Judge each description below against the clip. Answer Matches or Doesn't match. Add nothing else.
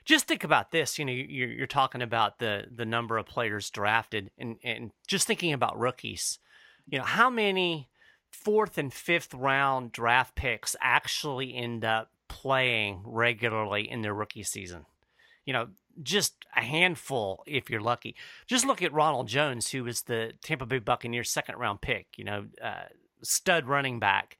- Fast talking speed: Doesn't match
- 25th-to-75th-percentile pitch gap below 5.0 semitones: Doesn't match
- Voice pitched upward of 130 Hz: Doesn't match